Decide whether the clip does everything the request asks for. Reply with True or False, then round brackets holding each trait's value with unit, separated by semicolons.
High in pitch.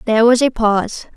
True (230 Hz)